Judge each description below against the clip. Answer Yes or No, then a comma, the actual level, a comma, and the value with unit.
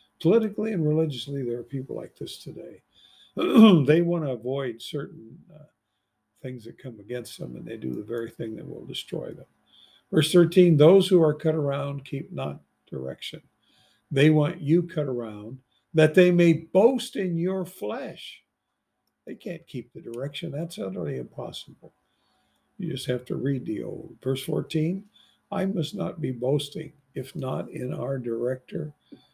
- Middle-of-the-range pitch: Yes, medium, 150 Hz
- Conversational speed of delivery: Yes, average, 160 wpm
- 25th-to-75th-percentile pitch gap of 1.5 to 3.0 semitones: No, average, 5.1 semitones